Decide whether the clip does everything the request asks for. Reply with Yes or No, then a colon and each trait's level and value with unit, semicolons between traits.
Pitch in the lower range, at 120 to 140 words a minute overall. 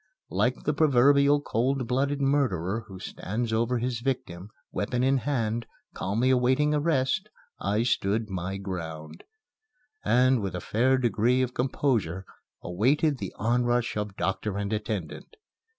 Yes: low, 120 Hz; slow, 135 wpm